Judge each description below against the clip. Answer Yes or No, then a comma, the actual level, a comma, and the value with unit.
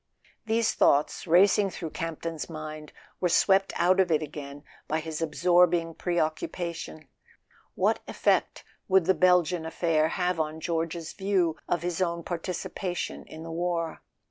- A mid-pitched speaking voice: Yes, medium, 170 Hz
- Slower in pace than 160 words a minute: Yes, average, 145 wpm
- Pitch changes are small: Yes, narrow, 2.2 semitones